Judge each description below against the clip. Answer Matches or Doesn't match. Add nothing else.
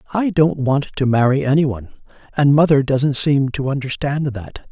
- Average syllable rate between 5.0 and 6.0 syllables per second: Matches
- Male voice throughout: Matches